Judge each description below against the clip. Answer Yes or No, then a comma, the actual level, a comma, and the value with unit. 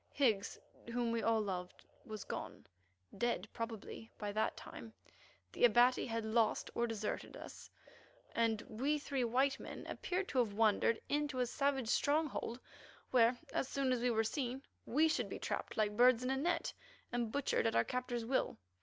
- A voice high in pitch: Yes, high, 240 Hz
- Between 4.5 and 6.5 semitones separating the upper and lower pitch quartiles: No, average, 3.1 semitones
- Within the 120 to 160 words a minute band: No, average, 170 wpm